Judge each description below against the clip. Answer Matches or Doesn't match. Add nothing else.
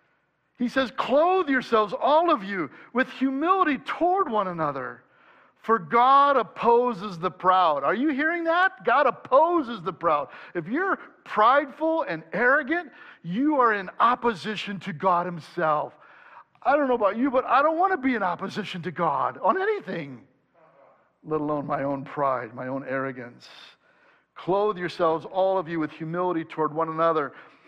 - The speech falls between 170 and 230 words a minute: Doesn't match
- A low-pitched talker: Doesn't match